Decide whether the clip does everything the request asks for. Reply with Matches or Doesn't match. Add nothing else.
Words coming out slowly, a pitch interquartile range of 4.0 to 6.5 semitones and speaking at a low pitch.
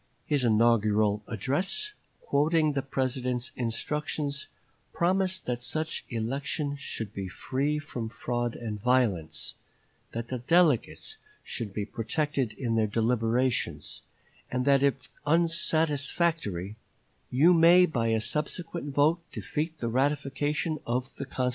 Matches